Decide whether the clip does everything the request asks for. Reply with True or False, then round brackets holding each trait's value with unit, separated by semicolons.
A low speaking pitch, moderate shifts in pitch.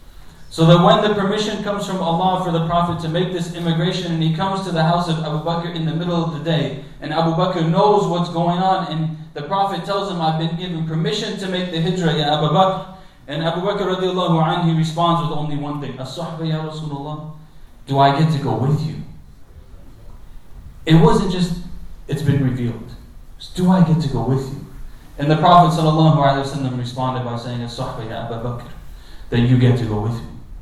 False (160 Hz; 4.5 semitones)